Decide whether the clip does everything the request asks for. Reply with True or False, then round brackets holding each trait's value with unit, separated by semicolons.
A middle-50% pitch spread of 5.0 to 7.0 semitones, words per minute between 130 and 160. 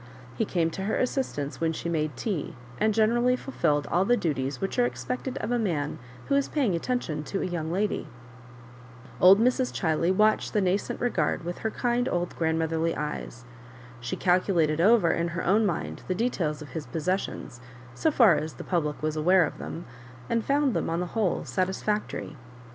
False (5.6 semitones; 185 wpm)